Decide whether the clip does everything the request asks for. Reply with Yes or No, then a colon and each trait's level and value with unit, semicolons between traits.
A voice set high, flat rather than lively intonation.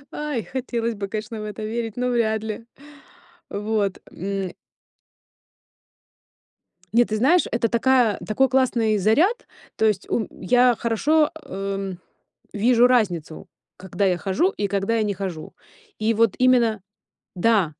No: high, 220 Hz; average, 3.4 semitones